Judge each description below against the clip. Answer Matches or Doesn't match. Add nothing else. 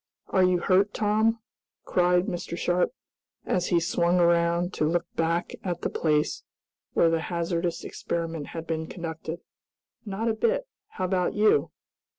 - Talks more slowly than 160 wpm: Matches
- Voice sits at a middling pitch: Matches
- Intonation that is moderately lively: Doesn't match